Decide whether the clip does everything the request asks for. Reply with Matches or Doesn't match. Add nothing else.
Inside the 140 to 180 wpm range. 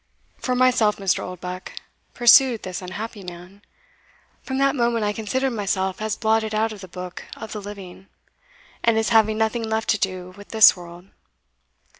Matches